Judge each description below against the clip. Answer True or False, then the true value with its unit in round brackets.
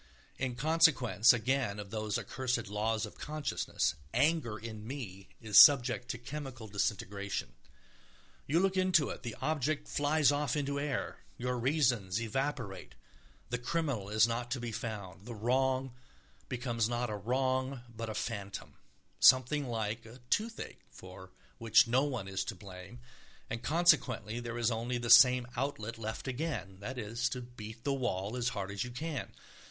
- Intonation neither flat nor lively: True (3.7 semitones)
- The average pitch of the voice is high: False (120 Hz)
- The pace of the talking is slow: False (155 wpm)